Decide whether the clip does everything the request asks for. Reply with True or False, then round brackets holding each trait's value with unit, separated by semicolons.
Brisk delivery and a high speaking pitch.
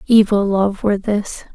False (155 wpm; 205 Hz)